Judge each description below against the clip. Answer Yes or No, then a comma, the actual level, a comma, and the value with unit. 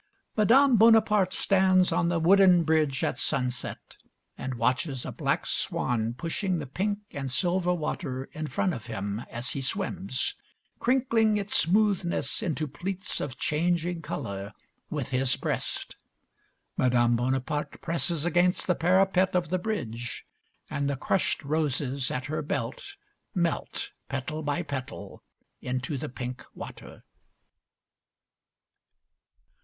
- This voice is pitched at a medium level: Yes, medium, 155 Hz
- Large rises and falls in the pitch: Yes, wide, 6.1 semitones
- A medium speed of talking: No, slow, 125 wpm